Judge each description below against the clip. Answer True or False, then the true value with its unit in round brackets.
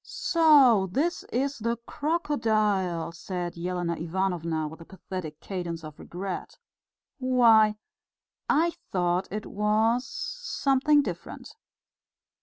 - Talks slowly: True (100 wpm)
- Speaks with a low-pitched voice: False (210 Hz)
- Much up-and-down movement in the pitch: True (6.8 semitones)